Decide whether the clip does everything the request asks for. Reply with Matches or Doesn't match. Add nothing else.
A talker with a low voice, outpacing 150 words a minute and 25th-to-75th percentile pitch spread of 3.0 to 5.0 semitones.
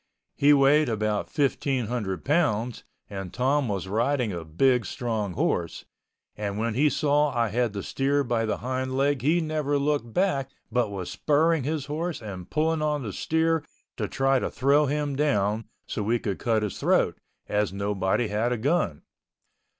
Doesn't match